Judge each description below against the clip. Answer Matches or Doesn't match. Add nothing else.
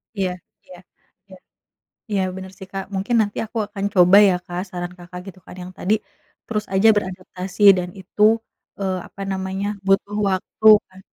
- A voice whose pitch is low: Doesn't match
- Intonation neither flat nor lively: Doesn't match